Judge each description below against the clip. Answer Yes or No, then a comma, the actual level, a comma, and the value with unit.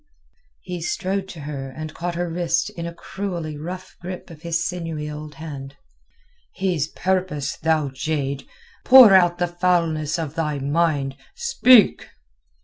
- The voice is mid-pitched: Yes, medium, 165 Hz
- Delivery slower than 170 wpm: Yes, average, 140 wpm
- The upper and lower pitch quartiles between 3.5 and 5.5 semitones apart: No, average, 3.0 semitones